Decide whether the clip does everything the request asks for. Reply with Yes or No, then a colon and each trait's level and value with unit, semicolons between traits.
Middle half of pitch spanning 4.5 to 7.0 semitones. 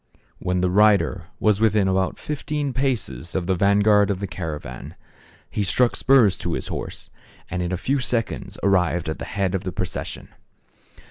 No: average, 3.3 semitones